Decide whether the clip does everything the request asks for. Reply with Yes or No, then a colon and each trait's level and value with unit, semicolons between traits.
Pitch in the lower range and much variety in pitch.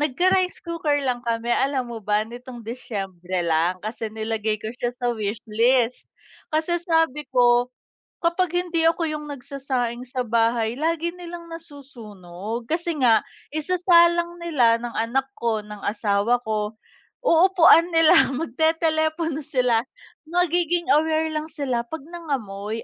No: very high, 260 Hz; wide, 6.4 semitones